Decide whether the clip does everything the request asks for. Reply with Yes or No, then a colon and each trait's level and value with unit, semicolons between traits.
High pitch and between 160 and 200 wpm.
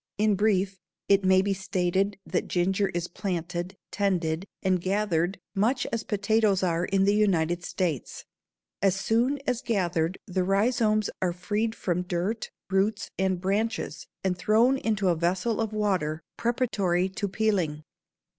No: high, 195 Hz; average, 145 wpm